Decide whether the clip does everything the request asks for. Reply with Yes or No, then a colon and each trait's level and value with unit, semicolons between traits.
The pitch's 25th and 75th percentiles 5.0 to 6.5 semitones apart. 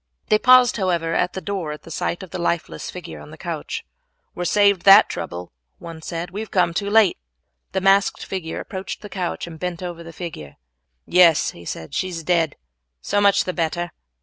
No: average, 2.9 semitones